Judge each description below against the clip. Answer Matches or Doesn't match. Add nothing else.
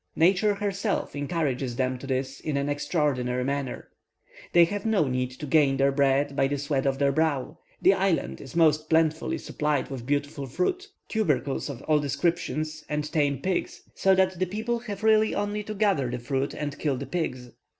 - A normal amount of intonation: Matches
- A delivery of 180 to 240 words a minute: Matches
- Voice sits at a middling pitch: Matches